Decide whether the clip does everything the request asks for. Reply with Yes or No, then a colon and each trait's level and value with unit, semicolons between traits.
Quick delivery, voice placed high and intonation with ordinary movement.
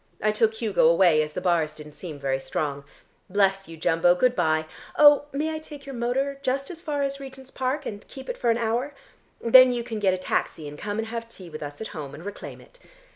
No: fast, 235 wpm; high, 220 Hz; wide, 8.4 semitones